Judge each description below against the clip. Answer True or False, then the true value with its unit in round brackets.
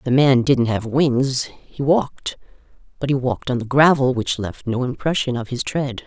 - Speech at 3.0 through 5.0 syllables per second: True (4.8 syllables/s)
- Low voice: True (130 Hz)